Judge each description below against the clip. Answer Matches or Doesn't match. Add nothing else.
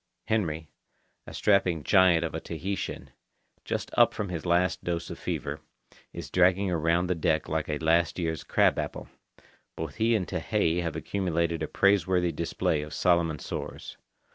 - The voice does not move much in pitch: Matches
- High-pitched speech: Doesn't match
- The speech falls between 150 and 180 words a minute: Matches